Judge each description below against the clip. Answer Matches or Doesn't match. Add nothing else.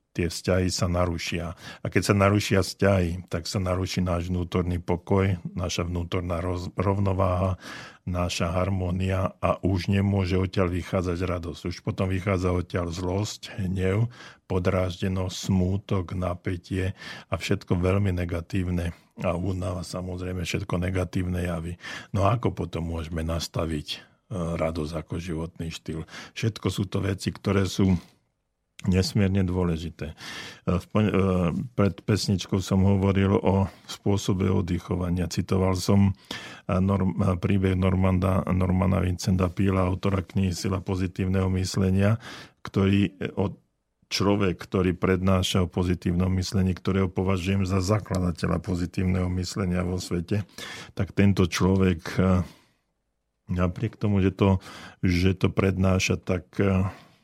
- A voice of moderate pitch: Doesn't match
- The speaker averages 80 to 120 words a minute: Matches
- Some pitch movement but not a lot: Doesn't match